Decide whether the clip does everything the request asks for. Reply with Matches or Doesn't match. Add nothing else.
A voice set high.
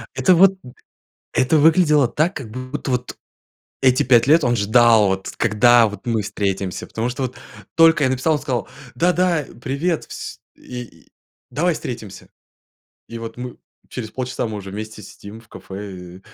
Doesn't match